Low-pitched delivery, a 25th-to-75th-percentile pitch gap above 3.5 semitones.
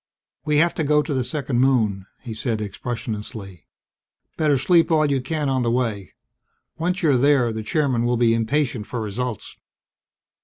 Yes: low, 125 Hz; average, 4.8 semitones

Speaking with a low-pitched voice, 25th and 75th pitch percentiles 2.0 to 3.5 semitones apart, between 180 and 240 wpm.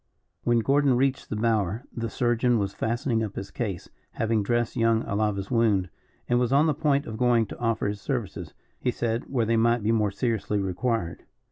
Yes: low, 115 Hz; narrow, 2.5 semitones; average, 195 wpm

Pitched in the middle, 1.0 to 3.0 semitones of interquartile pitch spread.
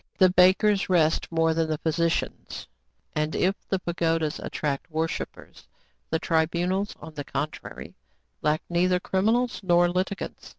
Yes: medium, 170 Hz; narrow, 2.6 semitones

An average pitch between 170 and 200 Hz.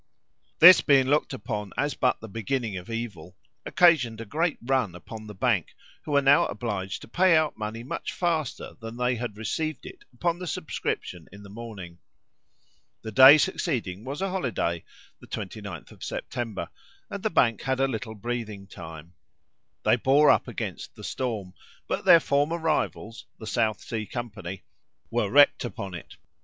No: low, 115 Hz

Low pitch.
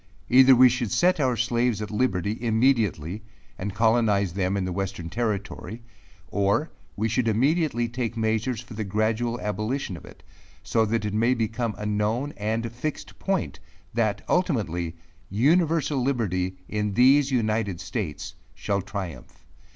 Yes: low, 110 Hz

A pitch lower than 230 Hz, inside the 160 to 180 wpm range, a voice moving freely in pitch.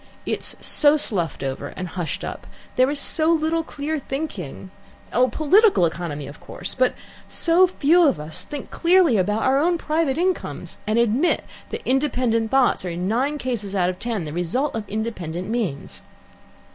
No: high, 240 Hz; average, 170 wpm; wide, 8.6 semitones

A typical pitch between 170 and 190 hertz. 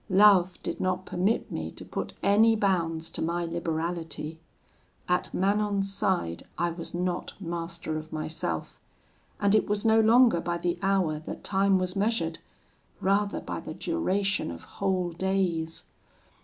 Yes: medium, 185 Hz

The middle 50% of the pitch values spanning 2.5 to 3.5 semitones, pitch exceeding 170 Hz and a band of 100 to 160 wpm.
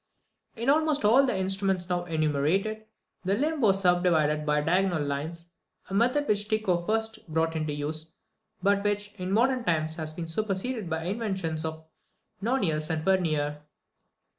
No: average, 5.2 semitones; medium, 185 Hz; average, 155 wpm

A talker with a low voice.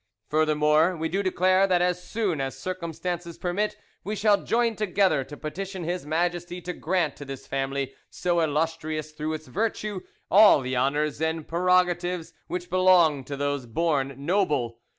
No: medium, 170 Hz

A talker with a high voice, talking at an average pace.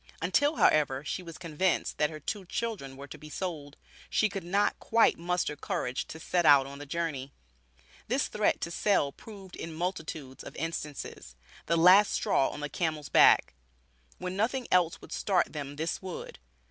No: medium, 165 Hz; average, 175 wpm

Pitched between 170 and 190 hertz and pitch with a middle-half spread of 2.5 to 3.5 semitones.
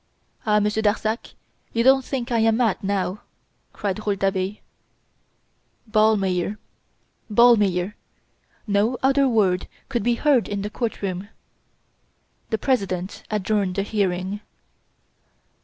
No: high, 210 Hz; average, 2.9 semitones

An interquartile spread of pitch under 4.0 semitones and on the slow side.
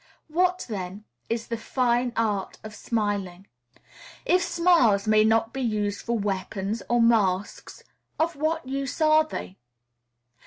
No: average, 4.9 semitones; slow, 130 wpm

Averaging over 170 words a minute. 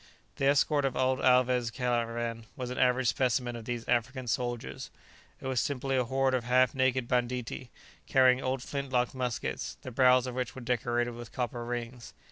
Yes: average, 180 wpm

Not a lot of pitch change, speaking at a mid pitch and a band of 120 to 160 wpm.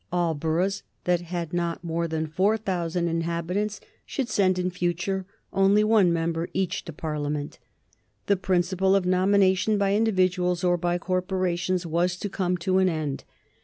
Yes: narrow, 2.2 semitones; medium, 180 Hz; average, 150 wpm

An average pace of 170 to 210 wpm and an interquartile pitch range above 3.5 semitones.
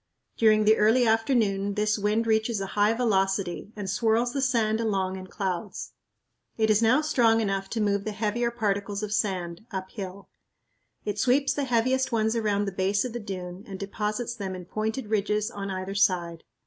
No: average, 180 wpm; narrow, 2.4 semitones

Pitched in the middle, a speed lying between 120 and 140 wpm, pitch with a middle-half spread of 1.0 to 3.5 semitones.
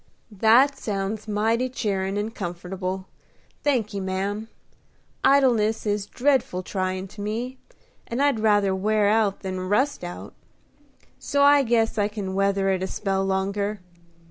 No: high, 205 Hz; slow, 135 wpm; average, 2.8 semitones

